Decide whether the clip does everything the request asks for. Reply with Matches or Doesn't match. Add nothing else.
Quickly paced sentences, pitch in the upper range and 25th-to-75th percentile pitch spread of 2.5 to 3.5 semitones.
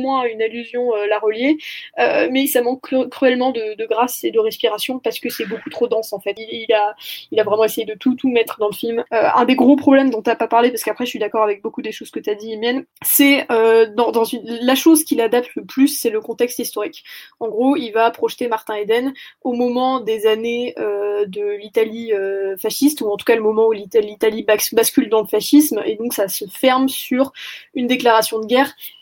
Matches